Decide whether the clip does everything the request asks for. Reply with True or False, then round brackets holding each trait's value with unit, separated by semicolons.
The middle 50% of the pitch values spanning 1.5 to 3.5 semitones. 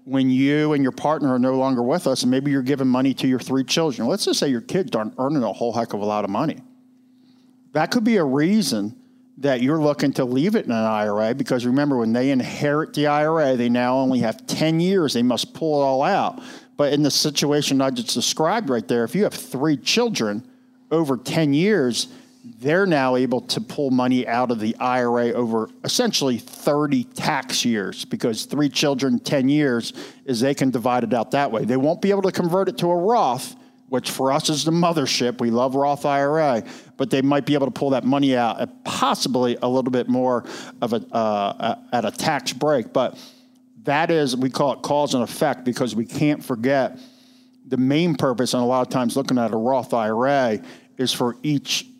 False (4.6 semitones)